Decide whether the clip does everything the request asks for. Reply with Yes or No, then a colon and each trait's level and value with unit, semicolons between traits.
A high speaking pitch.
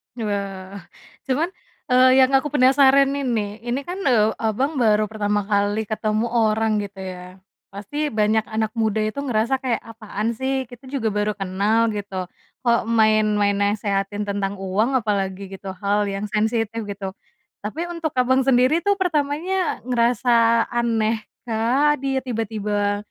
Yes: high, 220 Hz